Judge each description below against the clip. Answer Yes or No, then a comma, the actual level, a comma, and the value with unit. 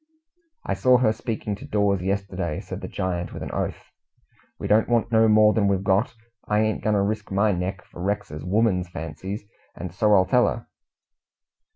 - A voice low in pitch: Yes, low, 100 Hz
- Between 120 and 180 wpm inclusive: No, average, 190 wpm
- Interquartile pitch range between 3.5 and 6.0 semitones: No, average, 2.7 semitones